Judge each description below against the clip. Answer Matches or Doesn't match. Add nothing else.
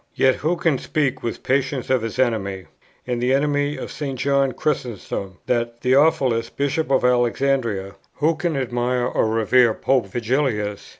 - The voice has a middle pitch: Doesn't match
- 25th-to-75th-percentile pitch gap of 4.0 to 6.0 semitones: Doesn't match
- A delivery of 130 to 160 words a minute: Matches